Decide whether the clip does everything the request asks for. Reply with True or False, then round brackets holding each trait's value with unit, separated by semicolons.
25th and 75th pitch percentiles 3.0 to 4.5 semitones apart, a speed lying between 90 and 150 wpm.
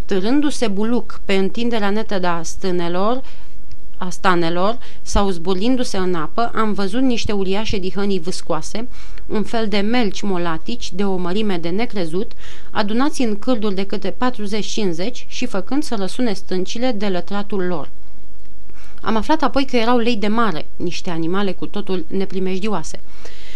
True (3.9 semitones; 145 wpm)